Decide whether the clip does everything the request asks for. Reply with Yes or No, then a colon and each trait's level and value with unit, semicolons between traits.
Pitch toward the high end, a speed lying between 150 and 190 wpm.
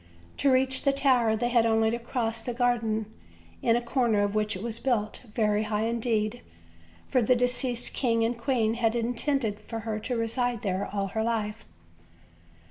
Yes: high, 230 Hz; average, 175 wpm